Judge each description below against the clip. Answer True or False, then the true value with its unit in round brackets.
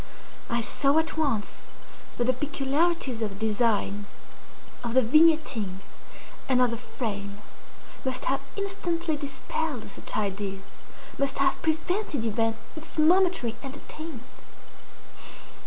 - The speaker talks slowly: True (110 wpm)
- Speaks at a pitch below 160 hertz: False (260 Hz)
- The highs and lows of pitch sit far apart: True (6.0 semitones)